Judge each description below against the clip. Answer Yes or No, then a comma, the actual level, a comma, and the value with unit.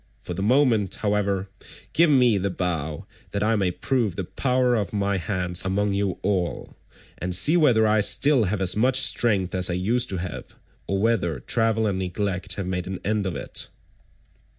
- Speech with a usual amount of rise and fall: Yes, average, 3.5 semitones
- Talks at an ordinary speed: Yes, average, 185 wpm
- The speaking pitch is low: Yes, low, 100 Hz